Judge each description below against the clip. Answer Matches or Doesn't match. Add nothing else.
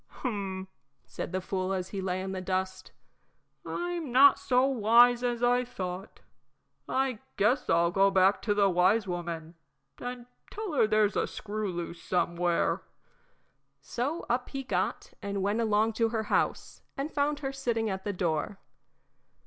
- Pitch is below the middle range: Doesn't match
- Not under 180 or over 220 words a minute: Doesn't match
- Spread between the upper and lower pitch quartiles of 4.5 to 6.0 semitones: Matches